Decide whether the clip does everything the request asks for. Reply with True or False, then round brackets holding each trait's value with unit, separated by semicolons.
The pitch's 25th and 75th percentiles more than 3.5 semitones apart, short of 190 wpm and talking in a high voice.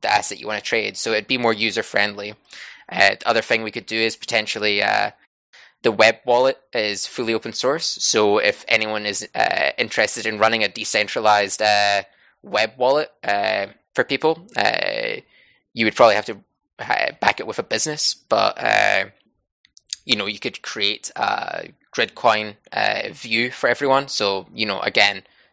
False (4.4 semitones; 170 wpm; 115 Hz)